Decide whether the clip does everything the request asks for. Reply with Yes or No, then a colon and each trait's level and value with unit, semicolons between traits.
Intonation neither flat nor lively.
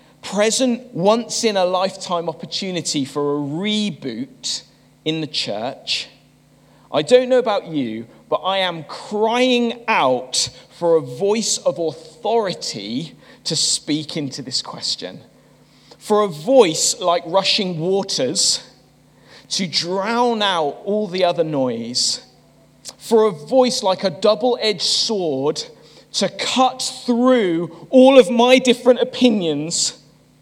No: wide, 6.5 semitones